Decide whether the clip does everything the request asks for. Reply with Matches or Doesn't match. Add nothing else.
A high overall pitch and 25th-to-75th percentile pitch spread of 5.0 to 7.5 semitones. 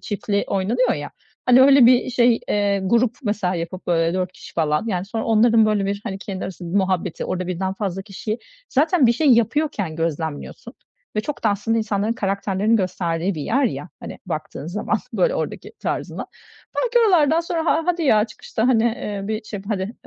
Doesn't match